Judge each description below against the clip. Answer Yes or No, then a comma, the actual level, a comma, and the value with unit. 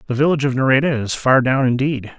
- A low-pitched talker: Yes, low, 130 Hz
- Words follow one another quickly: Yes, fast, 220 wpm